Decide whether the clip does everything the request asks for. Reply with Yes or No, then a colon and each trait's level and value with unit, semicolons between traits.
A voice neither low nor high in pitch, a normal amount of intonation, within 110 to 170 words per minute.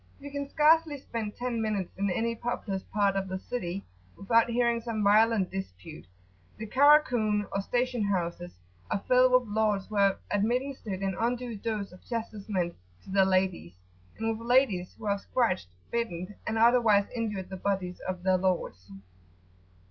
No: high, 210 Hz; average, 3.7 semitones; average, 160 wpm